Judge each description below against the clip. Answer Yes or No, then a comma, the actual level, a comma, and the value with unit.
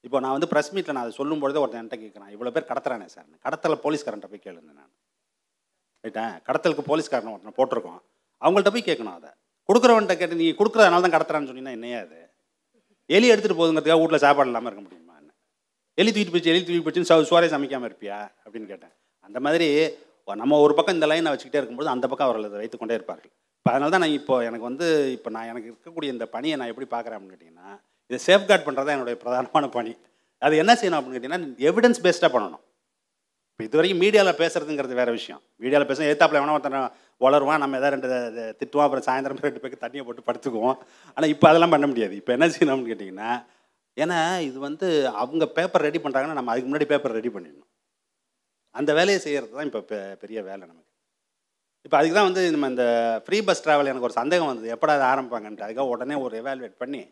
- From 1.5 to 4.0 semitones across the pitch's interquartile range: No, wide, 5.6 semitones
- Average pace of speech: No, fast, 190 wpm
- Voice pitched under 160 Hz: Yes, medium, 140 Hz